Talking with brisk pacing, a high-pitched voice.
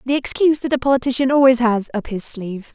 Yes: fast, 220 wpm; very high, 250 Hz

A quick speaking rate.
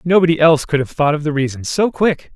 Yes: fast, 255 wpm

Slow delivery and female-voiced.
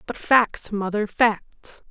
Yes: slow, 125 wpm; female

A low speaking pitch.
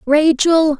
No: very high, 300 Hz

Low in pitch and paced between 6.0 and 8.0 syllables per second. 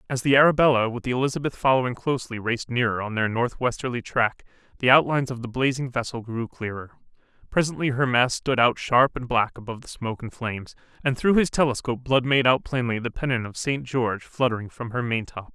Yes: low, 125 Hz; 6.2 syllables/s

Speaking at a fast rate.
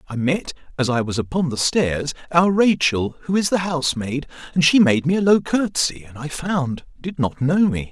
Yes: fast, 220 wpm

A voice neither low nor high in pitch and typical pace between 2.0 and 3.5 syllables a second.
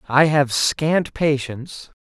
Yes: medium, 145 Hz; 3.4 syllables/s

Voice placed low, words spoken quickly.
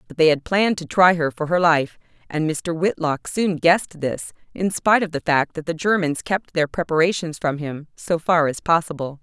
No: medium, 165 Hz; fast, 215 wpm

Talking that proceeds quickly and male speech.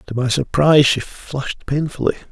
No: average, 155 wpm; male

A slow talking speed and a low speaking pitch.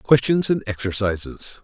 Yes: slow, 110 wpm; low, 115 Hz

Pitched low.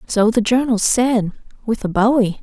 No: high, 225 Hz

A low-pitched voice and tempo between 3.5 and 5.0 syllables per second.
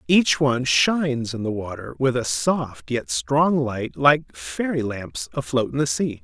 Yes: low, 130 Hz; 4.0 syllables/s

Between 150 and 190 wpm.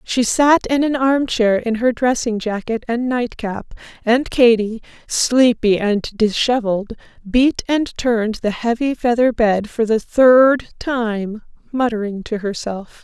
No: average, 140 wpm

